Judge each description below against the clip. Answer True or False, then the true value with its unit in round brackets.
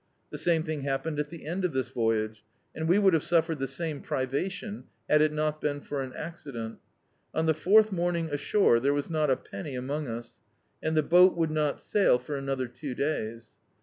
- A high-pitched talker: False (150 Hz)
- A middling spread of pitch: True (3.6 semitones)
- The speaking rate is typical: False (215 wpm)